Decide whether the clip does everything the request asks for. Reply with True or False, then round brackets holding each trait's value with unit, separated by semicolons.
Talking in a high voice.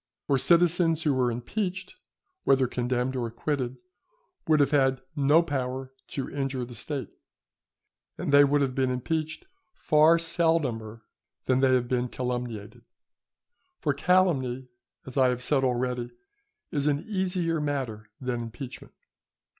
False (135 Hz)